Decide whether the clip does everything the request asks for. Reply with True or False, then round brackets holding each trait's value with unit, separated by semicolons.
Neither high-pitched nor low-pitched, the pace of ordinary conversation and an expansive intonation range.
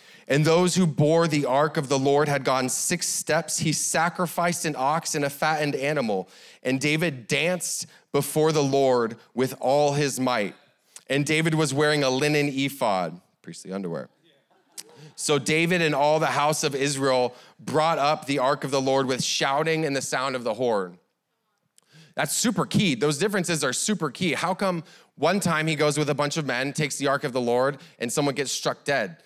False (150 Hz; 190 wpm; 2.9 semitones)